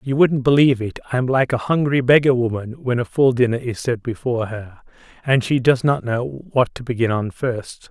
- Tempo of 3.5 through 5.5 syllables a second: Yes, 5.1 syllables/s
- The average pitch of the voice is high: No, low, 125 Hz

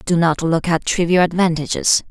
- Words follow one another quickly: No, average, 170 wpm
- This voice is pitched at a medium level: Yes, medium, 170 Hz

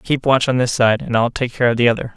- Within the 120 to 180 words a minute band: No, fast, 335 wpm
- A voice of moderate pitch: No, low, 120 Hz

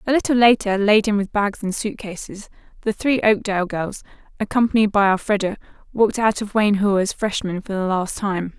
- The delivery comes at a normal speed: Yes, average, 190 wpm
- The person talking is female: Yes, female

